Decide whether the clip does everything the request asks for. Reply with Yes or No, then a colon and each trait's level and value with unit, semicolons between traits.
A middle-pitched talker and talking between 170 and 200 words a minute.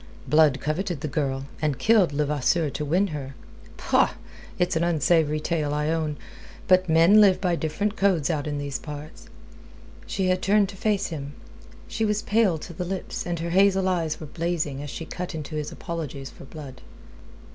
Yes: medium, 160 Hz; average, 180 wpm